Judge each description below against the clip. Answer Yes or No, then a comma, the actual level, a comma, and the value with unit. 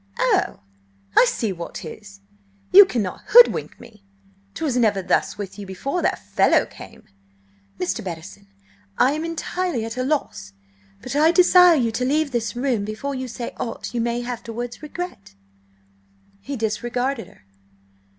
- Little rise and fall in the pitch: No, wide, 5.4 semitones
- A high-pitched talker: Yes, high, 240 Hz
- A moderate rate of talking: Yes, average, 150 wpm